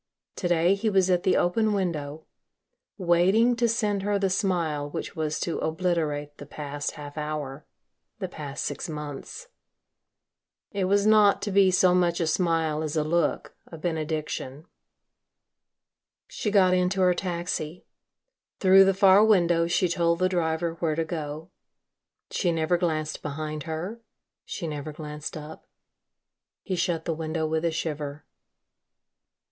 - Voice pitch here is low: No, medium, 170 Hz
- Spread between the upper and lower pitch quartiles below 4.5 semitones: Yes, average, 3.2 semitones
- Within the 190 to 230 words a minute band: No, average, 145 wpm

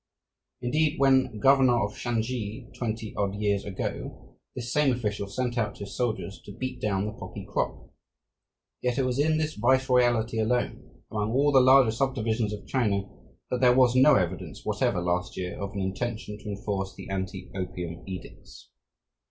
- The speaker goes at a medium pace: Yes, average, 165 wpm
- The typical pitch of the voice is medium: No, low, 115 Hz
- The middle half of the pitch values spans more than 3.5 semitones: Yes, average, 4.1 semitones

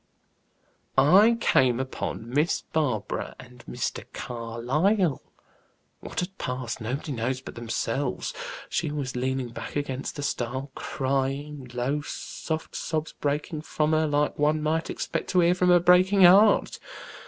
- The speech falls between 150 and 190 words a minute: No, slow, 135 wpm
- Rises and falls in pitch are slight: No, average, 4.0 semitones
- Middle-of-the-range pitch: Yes, medium, 145 Hz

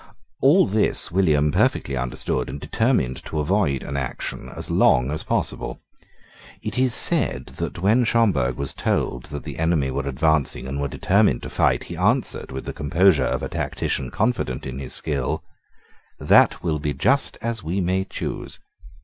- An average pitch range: No, wide, 6.5 semitones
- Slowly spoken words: No, average, 165 wpm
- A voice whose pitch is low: Yes, very low, 75 Hz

